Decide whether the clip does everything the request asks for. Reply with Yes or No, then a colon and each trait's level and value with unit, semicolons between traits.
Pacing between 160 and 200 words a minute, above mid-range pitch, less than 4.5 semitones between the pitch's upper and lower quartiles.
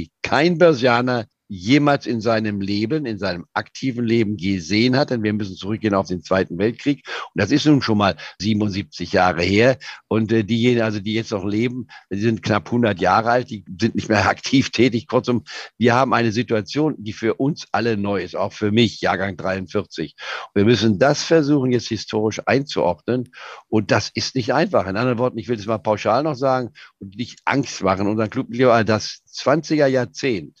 No: fast, 190 wpm; low, 115 Hz; average, 3.5 semitones